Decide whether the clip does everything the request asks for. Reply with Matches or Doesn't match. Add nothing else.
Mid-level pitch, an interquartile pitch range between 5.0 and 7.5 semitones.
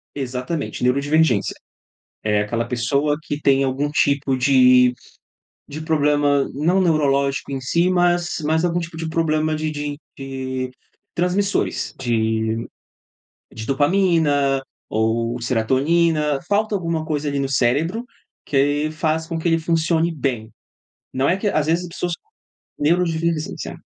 Doesn't match